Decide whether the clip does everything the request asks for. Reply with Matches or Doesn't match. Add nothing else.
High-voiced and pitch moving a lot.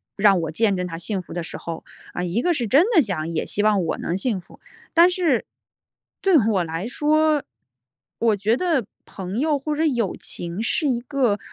Matches